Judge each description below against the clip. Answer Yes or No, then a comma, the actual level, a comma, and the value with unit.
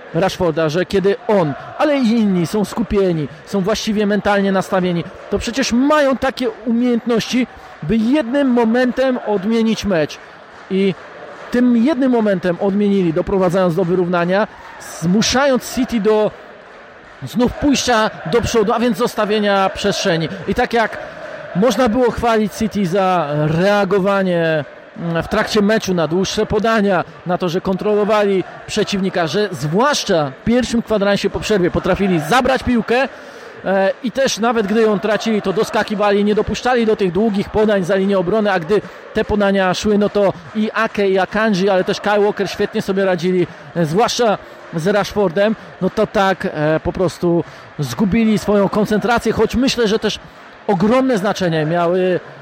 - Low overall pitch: No, high, 205 Hz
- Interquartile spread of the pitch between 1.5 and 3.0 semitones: No, average, 3.4 semitones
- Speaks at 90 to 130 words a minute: No, average, 145 wpm